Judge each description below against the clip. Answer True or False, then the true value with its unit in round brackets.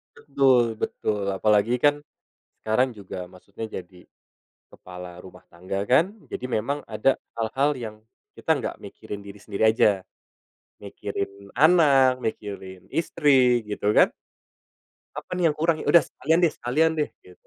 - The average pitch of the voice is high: False (110 Hz)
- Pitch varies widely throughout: True (5.7 semitones)